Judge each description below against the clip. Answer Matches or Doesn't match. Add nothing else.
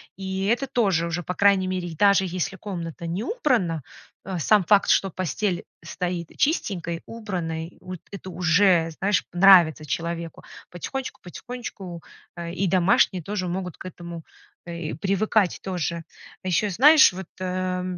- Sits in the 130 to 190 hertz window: Matches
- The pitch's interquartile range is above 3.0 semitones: Doesn't match